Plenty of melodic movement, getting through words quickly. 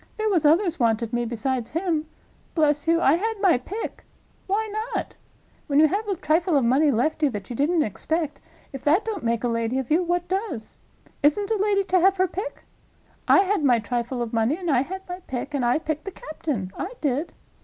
Yes: wide, 7.0 semitones; fast, 210 wpm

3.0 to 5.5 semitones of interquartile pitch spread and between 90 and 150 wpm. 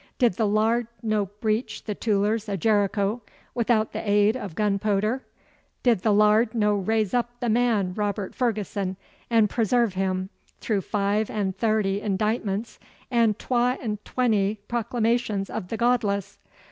No: narrow, 2.4 semitones; average, 145 wpm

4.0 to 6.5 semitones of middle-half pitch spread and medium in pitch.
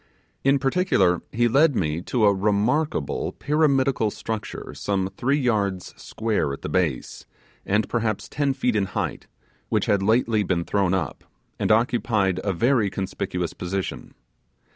No: average, 4.8 semitones; low, 105 Hz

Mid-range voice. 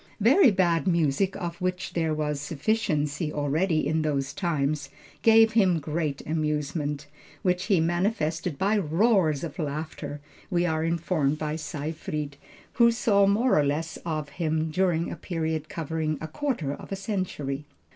Yes: medium, 160 Hz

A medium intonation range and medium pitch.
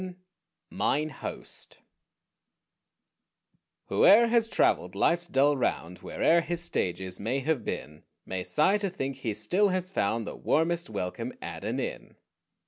No: wide, 8.9 semitones; medium, 150 Hz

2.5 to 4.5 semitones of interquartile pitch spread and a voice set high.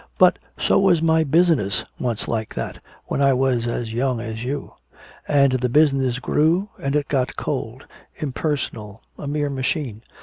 No: average, 3.8 semitones; low, 135 Hz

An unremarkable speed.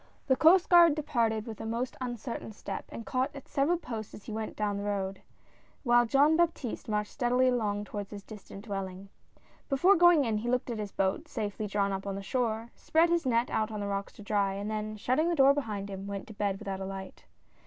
No: fast, 230 wpm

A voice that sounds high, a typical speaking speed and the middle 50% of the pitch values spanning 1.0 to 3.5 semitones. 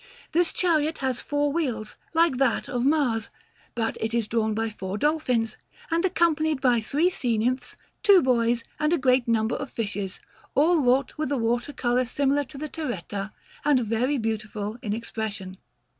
No: very high, 250 Hz; average, 170 wpm; average, 4.7 semitones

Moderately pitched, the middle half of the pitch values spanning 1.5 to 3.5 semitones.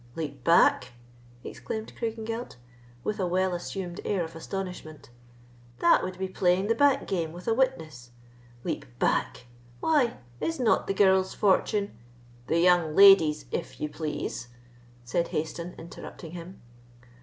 No: medium, 180 Hz; average, 4.1 semitones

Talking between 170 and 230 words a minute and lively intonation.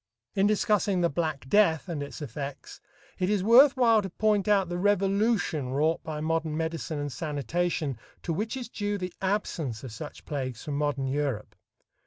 Yes: average, 175 wpm; wide, 5.9 semitones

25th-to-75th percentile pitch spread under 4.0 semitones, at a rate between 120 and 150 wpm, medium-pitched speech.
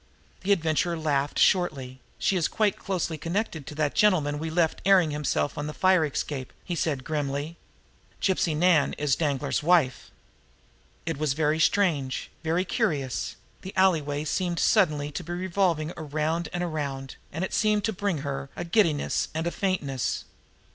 No: average, 3.6 semitones; average, 160 wpm; medium, 160 Hz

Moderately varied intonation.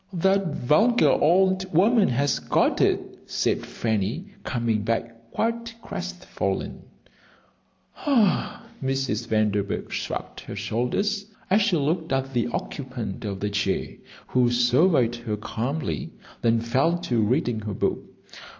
No: wide, 8.1 semitones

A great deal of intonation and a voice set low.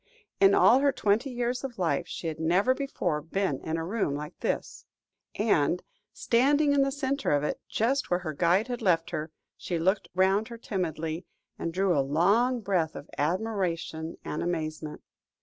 No: wide, 6.5 semitones; medium, 185 Hz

